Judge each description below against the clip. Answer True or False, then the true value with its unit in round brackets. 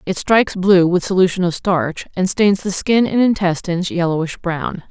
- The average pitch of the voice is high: False (180 Hz)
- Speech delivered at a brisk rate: False (185 wpm)